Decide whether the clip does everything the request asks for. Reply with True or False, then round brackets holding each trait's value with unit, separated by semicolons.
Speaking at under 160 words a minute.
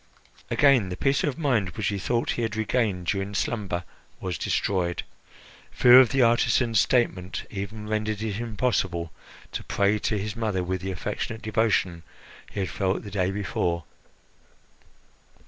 True (150 wpm)